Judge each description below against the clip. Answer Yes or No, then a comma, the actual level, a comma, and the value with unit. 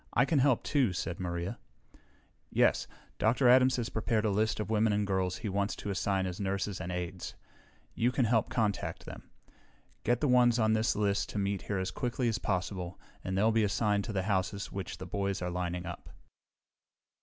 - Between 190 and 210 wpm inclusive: Yes, average, 195 wpm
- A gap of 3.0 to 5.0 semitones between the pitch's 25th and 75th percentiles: Yes, average, 3.3 semitones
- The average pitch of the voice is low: Yes, low, 100 Hz